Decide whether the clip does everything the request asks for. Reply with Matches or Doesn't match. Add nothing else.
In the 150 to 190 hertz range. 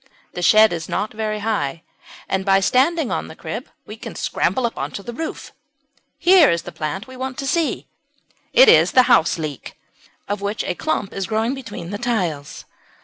Doesn't match